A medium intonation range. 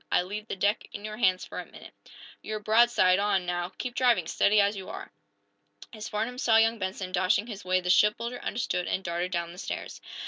Yes: average, 3.4 semitones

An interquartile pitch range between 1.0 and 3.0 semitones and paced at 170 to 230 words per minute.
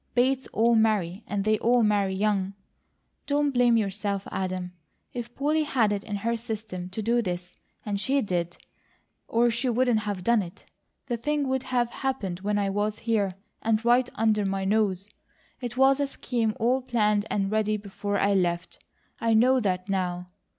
No: average, 3.5 semitones; average, 175 wpm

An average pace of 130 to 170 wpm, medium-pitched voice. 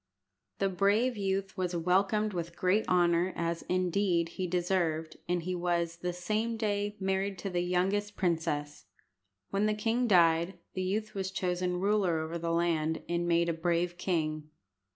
Yes: average, 160 wpm; medium, 180 Hz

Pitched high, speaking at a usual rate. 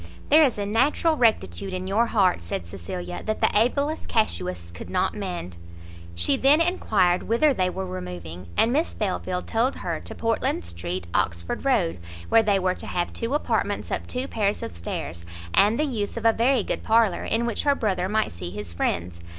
Yes: high, 195 Hz; average, 190 wpm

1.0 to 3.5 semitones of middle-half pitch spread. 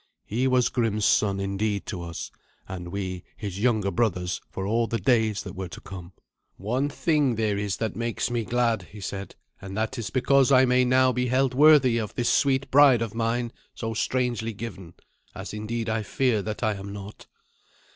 No: average, 3.9 semitones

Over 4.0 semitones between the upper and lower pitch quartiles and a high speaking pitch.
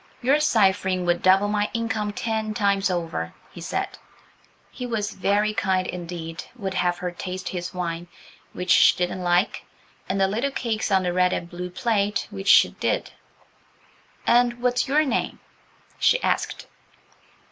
No: average, 3.6 semitones; high, 195 Hz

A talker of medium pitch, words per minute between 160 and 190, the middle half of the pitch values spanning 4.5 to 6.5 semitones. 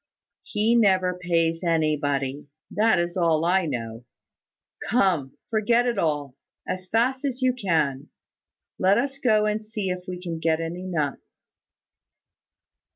No: medium, 180 Hz; slow, 135 wpm; average, 5.3 semitones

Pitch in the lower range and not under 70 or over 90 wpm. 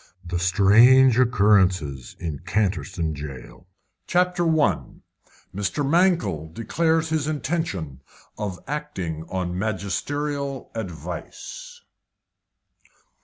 Yes: low, 105 Hz; slow, 80 wpm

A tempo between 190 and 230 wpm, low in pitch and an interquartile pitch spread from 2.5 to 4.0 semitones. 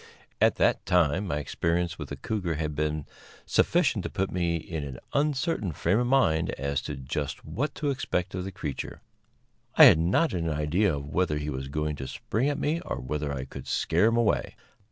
No: average, 195 wpm; very low, 85 Hz; average, 5.3 semitones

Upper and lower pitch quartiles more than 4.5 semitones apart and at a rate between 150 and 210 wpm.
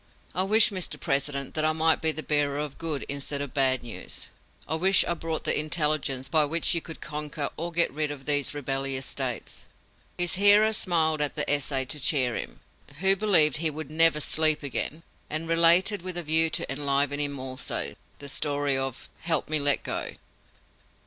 No: average, 2.7 semitones; average, 190 wpm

